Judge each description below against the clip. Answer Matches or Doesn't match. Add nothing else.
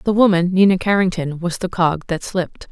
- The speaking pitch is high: Doesn't match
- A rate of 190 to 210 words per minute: Matches